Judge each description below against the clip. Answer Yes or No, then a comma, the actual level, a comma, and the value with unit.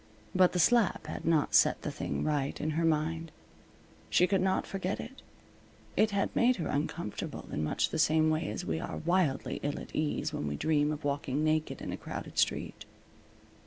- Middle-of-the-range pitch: Yes, medium, 155 Hz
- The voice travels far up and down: No, average, 3.6 semitones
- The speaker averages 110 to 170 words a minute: No, average, 195 wpm